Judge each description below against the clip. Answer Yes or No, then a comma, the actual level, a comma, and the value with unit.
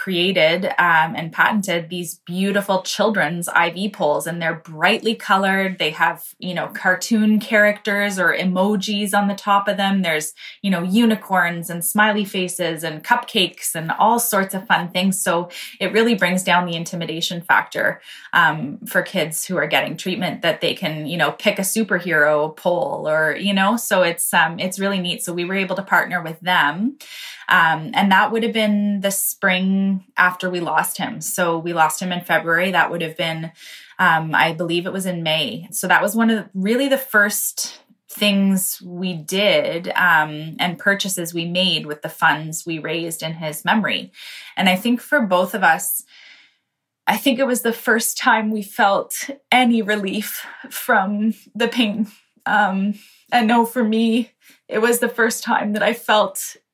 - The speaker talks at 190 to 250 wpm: No, average, 180 wpm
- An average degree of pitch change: Yes, average, 3.8 semitones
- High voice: Yes, high, 195 Hz